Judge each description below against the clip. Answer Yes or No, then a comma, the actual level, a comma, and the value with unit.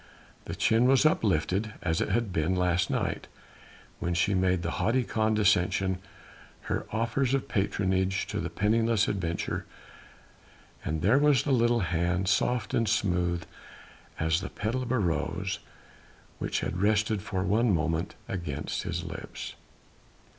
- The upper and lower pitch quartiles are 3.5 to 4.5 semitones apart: Yes, average, 4.2 semitones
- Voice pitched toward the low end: Yes, low, 100 Hz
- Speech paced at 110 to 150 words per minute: Yes, average, 140 wpm